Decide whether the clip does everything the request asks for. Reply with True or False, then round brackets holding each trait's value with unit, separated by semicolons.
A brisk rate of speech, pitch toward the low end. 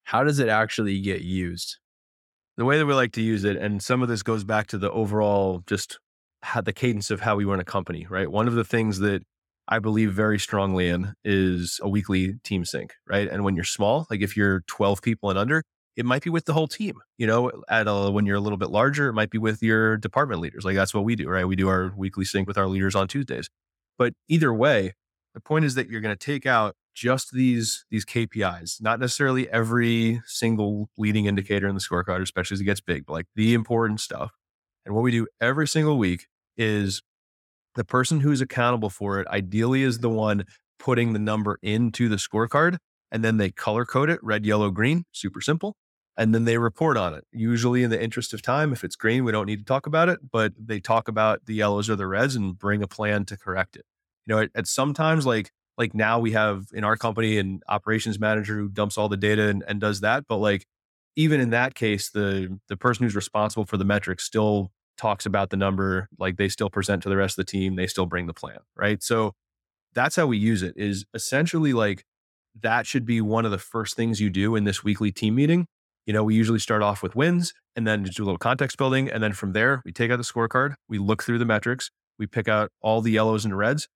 True (235 wpm; 110 Hz)